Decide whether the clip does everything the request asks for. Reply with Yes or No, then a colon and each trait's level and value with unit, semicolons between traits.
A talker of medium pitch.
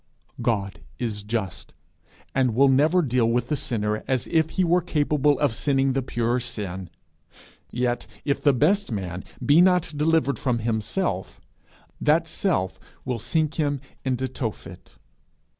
No: low, 130 Hz